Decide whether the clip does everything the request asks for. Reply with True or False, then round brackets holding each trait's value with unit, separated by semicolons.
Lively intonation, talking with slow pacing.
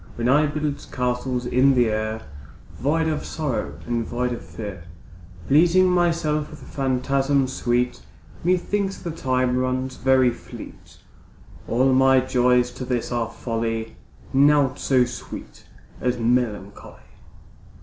False (2.9 semitones; 125 wpm)